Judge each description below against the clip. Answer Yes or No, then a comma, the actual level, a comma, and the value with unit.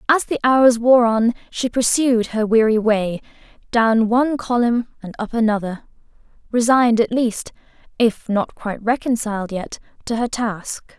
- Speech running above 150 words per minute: No, average, 145 wpm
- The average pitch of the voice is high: Yes, high, 230 Hz